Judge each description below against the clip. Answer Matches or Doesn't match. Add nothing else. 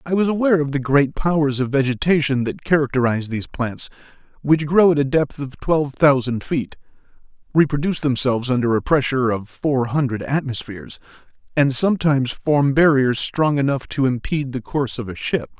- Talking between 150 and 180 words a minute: Matches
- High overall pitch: Doesn't match